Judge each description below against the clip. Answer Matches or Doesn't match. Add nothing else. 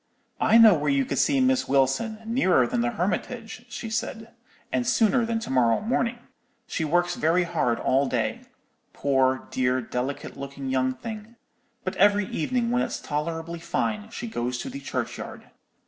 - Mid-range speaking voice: Matches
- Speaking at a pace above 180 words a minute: Doesn't match